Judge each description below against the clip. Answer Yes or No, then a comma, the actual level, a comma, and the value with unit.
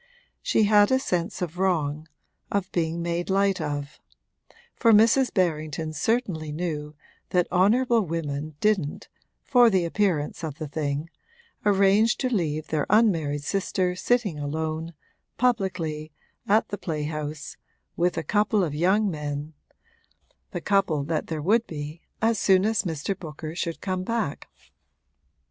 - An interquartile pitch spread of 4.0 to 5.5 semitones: Yes, average, 4.9 semitones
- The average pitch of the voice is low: No, medium, 175 Hz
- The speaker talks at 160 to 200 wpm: No, slow, 135 wpm